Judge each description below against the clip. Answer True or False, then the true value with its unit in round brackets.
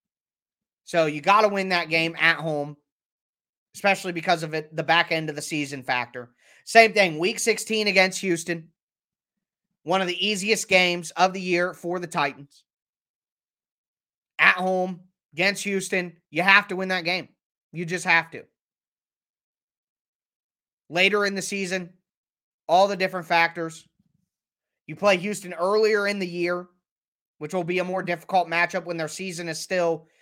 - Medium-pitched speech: True (180 Hz)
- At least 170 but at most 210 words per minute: False (155 wpm)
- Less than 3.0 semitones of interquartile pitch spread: True (2.5 semitones)